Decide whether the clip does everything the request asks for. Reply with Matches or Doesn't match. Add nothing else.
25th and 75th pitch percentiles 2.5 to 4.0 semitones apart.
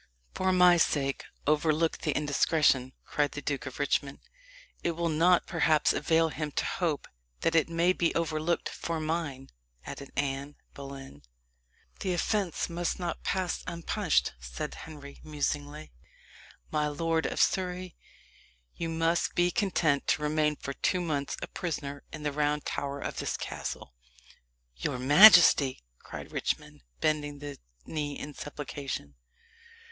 Matches